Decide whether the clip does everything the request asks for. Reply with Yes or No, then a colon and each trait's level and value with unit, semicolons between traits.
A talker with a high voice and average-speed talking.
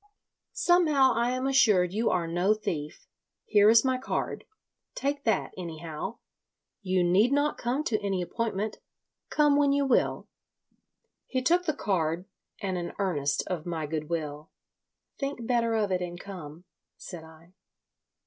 Yes: high, 200 Hz; average, 150 wpm